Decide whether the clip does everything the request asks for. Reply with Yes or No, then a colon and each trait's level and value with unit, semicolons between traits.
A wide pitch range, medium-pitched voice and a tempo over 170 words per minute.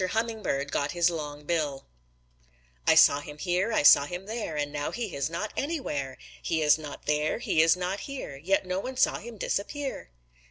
Yes: wide, 6.4 semitones; medium, 170 Hz; average, 190 wpm